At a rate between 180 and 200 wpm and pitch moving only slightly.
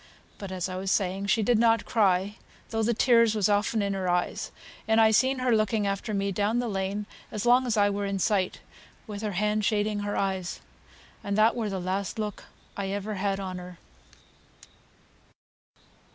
Yes: average, 190 wpm; narrow, 2.1 semitones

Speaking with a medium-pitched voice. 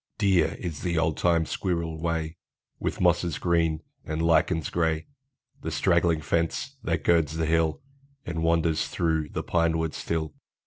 No: very low, 80 Hz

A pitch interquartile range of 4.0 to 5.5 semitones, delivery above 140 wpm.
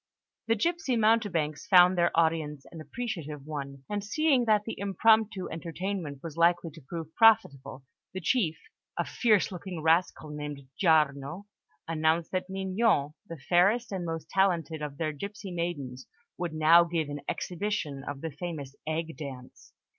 Yes: average, 4.7 semitones; average, 150 wpm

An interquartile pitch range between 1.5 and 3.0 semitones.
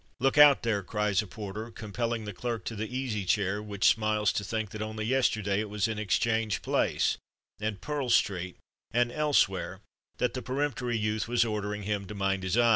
Yes: narrow, 2.5 semitones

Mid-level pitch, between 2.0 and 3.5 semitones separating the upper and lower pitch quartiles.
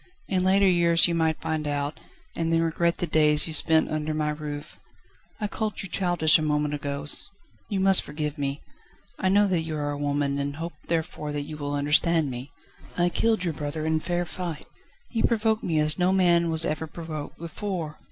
Yes: medium, 160 Hz; average, 2.9 semitones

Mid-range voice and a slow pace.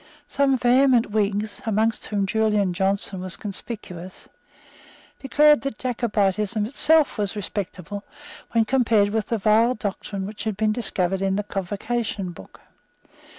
No: high, 210 Hz; slow, 130 wpm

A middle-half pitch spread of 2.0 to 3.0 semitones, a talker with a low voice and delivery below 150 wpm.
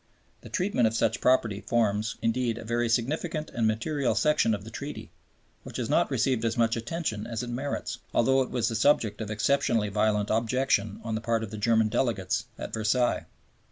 No: average, 2.7 semitones; low, 115 Hz; average, 190 wpm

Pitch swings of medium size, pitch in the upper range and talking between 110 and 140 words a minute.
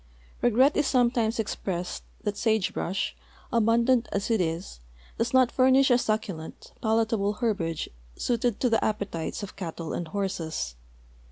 Yes: average, 4.2 semitones; high, 220 Hz; slow, 135 wpm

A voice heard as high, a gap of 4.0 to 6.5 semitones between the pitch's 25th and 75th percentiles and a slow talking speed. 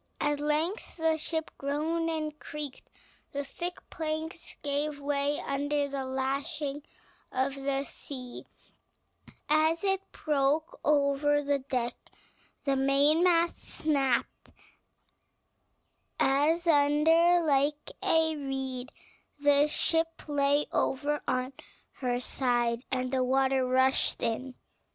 No: very high, 285 Hz; narrow, 2.4 semitones; slow, 105 wpm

